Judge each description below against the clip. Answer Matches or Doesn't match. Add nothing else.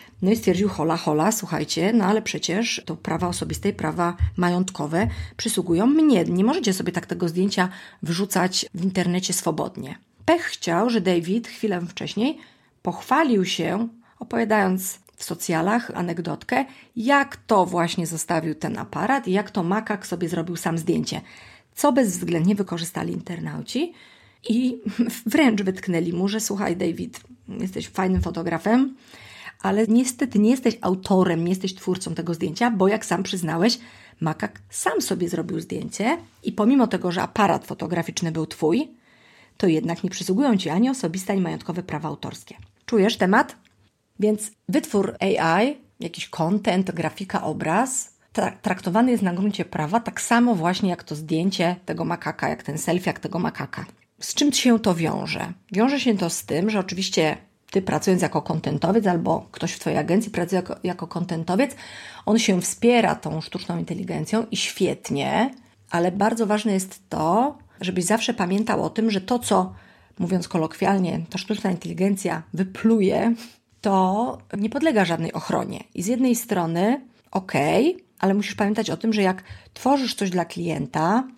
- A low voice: Doesn't match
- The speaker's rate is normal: Matches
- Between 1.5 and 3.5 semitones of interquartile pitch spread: Doesn't match